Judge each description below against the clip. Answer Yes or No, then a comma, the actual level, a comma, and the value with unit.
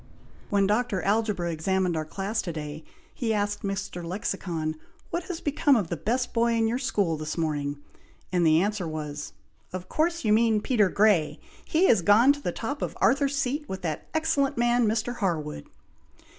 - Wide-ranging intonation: Yes, wide, 6.2 semitones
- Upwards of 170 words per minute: Yes, average, 180 wpm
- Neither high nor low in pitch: No, high, 205 Hz